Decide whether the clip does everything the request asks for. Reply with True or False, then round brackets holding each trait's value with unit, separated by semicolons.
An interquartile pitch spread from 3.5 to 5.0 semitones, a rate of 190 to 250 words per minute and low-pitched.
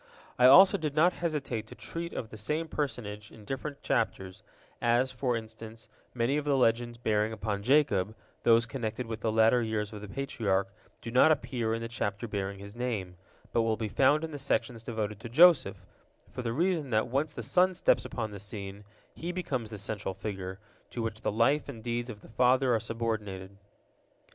True (4.1 semitones; 195 wpm; 115 Hz)